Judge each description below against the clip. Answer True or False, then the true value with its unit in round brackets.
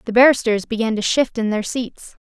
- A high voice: True (230 Hz)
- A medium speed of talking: False (210 wpm)